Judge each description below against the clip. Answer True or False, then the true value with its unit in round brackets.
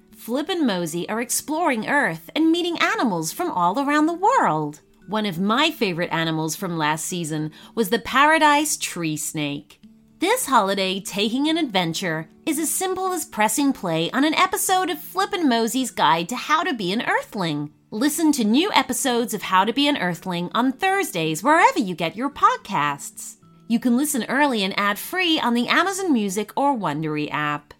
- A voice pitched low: False (235 Hz)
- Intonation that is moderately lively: False (9.0 semitones)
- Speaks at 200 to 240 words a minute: False (180 wpm)